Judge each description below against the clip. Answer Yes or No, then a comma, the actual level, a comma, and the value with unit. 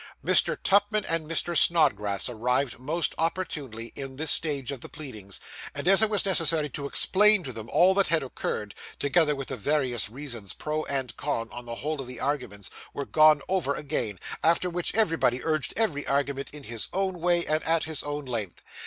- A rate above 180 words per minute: Yes, average, 190 wpm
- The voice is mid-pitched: Yes, medium, 145 Hz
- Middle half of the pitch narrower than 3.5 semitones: No, average, 4.7 semitones